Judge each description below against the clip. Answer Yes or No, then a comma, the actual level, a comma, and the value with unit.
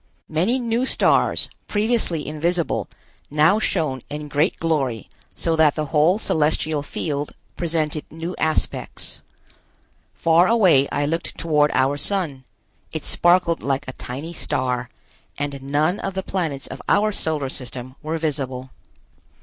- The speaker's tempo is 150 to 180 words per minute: No, slow, 135 wpm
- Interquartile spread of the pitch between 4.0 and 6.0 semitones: No, average, 3.3 semitones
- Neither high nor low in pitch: Yes, medium, 155 Hz